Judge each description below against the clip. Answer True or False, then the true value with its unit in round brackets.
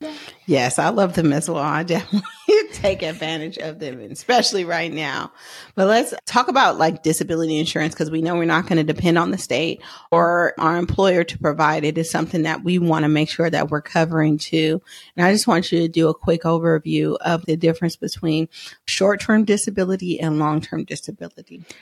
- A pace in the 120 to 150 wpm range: False (200 wpm)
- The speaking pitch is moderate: True (165 Hz)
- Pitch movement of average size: False (1.9 semitones)